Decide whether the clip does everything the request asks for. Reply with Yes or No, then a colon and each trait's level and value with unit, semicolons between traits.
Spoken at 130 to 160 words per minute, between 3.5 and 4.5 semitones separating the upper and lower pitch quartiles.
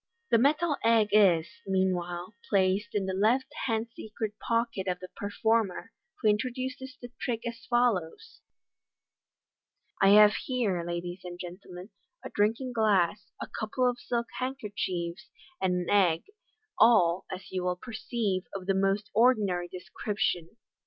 Yes: average, 140 wpm; average, 4.1 semitones